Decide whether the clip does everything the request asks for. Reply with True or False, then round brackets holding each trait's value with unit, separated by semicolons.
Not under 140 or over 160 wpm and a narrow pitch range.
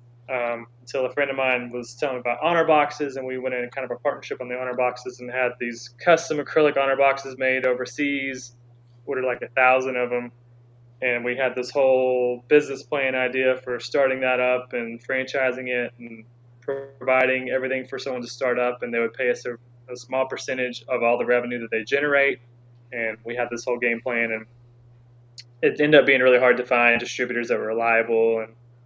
False (205 wpm; 1.5 semitones)